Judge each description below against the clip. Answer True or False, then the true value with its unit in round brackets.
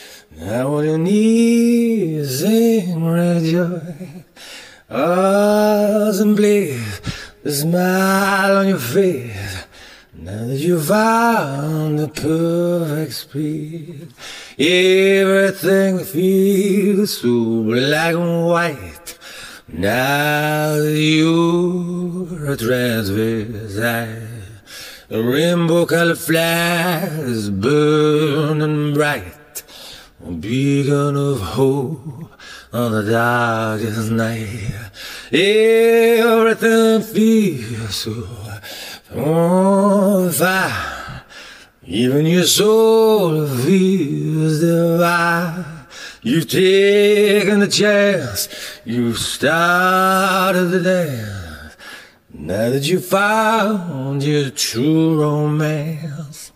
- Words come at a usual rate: False (75 wpm)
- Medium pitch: True (160 Hz)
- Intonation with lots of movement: True (6.3 semitones)